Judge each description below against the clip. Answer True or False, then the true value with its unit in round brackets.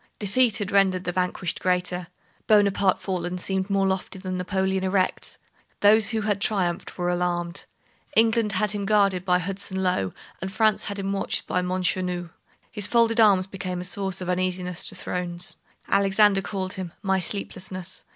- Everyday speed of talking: True (160 wpm)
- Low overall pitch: False (190 Hz)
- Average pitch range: False (1.8 semitones)